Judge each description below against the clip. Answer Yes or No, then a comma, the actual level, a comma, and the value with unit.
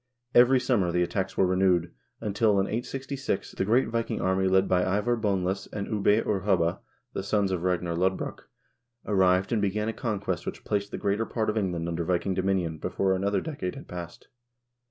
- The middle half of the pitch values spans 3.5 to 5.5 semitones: No, average, 2.7 semitones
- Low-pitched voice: Yes, very low, 95 Hz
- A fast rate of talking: No, average, 190 wpm